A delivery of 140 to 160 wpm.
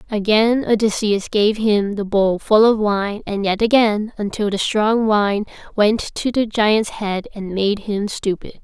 No: average, 175 wpm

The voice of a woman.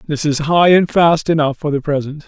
No: male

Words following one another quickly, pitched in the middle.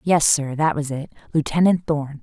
No: average, 160 wpm; medium, 150 Hz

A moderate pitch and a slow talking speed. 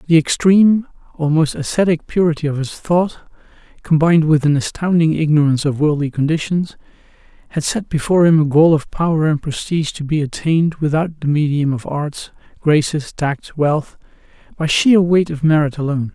No: medium, 155 Hz; average, 155 wpm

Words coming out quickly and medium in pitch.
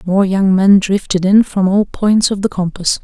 No: fast, 220 wpm; high, 195 Hz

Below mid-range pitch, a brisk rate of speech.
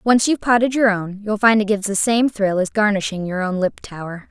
No: high, 205 Hz; fast, 235 wpm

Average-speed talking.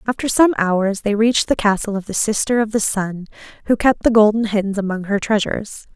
No: fast, 210 wpm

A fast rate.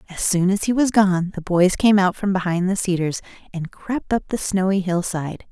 Yes: fast, 220 wpm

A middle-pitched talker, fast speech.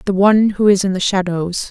No: high, 195 Hz; fast, 245 wpm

